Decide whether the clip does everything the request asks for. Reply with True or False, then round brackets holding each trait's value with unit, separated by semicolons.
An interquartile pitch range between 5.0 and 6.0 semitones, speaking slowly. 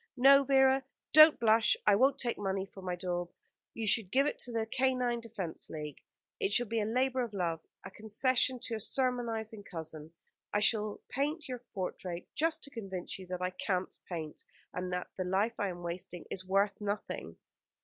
False (5.4 semitones; 190 wpm)